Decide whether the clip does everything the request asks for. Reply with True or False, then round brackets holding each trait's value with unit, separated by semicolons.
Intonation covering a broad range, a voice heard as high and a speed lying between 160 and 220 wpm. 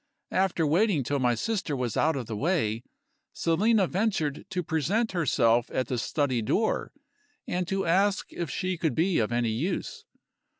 False (7.1 semitones; 160 Hz; 165 wpm)